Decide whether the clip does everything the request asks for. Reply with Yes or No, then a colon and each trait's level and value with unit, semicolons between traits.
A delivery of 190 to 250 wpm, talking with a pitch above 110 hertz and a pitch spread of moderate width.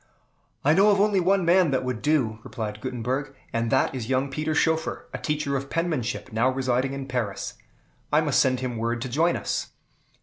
Yes: average, 195 wpm; low, 135 Hz; average, 4.3 semitones